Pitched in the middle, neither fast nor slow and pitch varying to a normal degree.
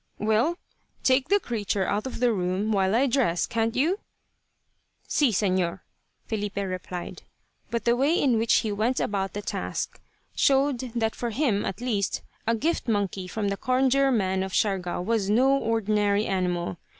No: high, 220 Hz; average, 160 wpm; average, 4.5 semitones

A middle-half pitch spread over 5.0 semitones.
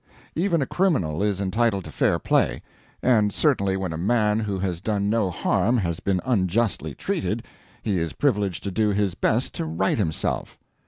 No: average, 3.5 semitones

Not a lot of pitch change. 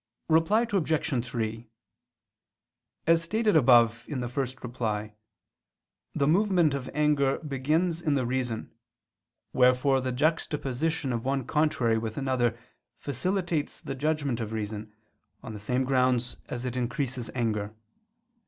No: average, 4.3 semitones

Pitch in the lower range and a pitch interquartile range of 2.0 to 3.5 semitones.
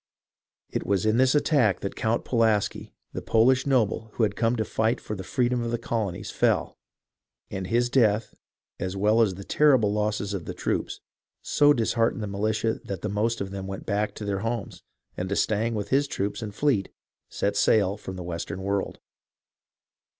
Yes: low, 110 Hz; average, 2.8 semitones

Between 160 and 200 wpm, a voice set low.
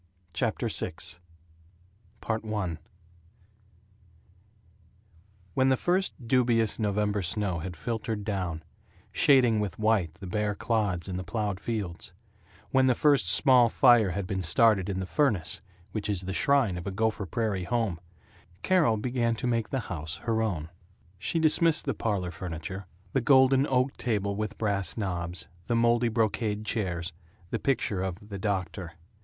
No: average, 145 wpm; low, 105 Hz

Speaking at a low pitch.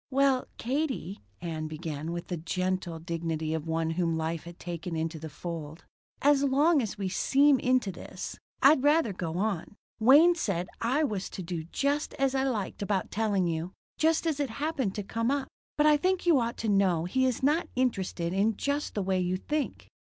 No: high, 200 Hz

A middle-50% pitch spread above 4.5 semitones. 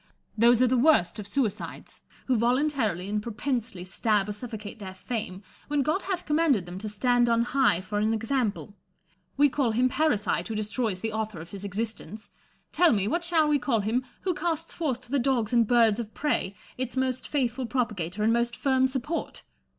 No: average, 4.1 semitones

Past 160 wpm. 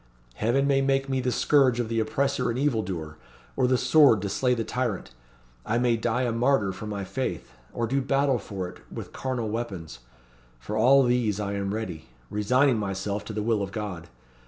Yes: average, 200 wpm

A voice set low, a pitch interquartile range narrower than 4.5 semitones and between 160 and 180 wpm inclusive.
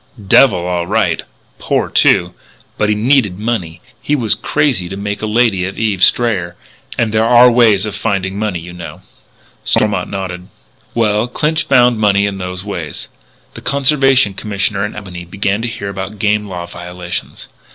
Yes: low, 105 Hz; average, 4.0 semitones; average, 165 wpm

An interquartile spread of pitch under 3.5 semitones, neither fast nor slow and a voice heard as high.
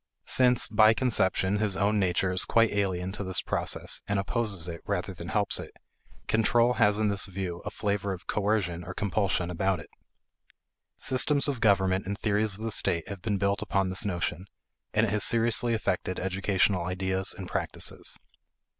No: narrow, 2.5 semitones; average, 175 wpm; low, 100 Hz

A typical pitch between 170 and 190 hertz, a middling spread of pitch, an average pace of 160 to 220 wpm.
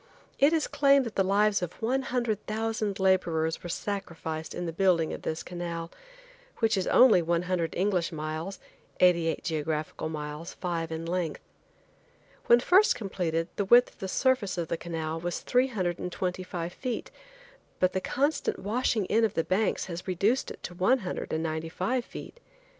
Yes: medium, 185 Hz; average, 4.8 semitones; average, 170 wpm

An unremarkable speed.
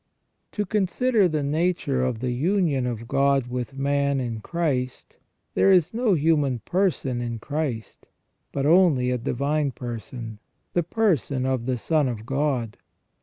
Yes: average, 145 wpm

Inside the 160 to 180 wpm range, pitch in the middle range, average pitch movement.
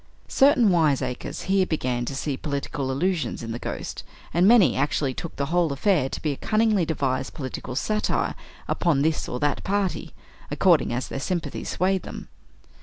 No: average, 170 wpm; medium, 155 Hz; wide, 5.8 semitones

